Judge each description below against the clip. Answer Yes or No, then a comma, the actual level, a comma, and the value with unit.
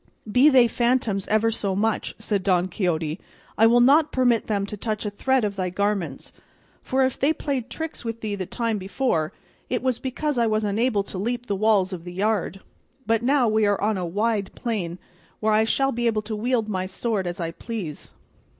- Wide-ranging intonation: No, average, 3.6 semitones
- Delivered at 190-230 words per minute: Yes, fast, 205 wpm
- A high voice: Yes, high, 215 Hz